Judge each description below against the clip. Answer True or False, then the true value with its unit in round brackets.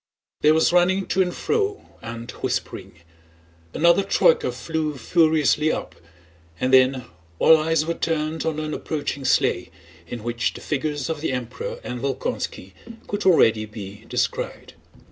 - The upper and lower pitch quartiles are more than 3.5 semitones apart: True (4.5 semitones)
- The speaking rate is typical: True (145 wpm)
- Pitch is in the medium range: True (155 Hz)